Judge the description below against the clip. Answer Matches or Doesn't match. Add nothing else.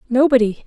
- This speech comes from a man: Doesn't match